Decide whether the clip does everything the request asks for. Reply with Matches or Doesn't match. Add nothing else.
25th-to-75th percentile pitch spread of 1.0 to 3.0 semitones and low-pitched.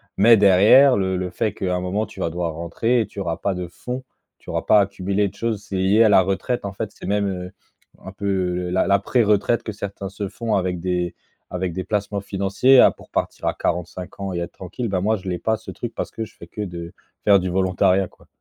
Matches